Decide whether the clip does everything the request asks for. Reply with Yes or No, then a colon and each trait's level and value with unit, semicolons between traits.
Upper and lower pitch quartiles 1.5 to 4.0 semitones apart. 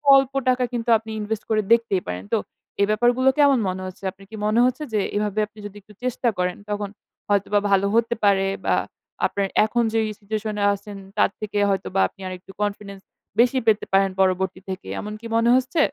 Yes: average, 2.9 semitones